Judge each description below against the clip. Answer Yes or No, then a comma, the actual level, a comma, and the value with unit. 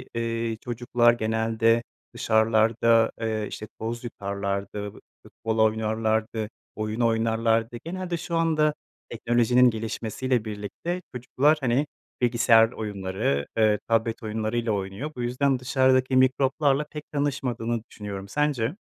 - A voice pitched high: No, low, 115 Hz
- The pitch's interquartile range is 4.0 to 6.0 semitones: No, average, 2.8 semitones